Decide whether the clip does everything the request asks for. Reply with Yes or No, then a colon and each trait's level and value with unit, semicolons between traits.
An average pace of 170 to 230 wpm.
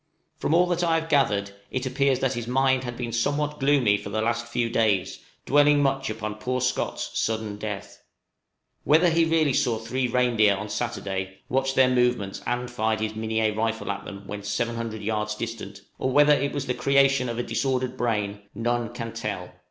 Yes: average, 190 wpm